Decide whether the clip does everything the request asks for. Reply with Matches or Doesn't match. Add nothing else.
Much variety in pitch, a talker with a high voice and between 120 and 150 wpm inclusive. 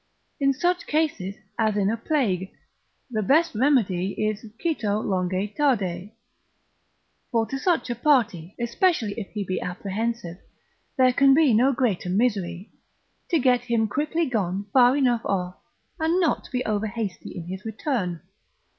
Matches